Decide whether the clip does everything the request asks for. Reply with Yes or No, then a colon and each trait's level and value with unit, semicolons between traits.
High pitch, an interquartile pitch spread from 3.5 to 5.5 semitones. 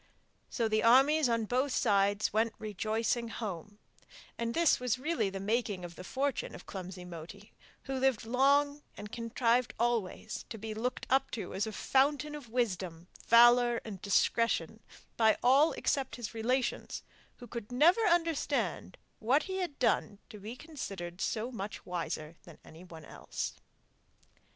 Yes: high, 230 Hz; average, 4.2 semitones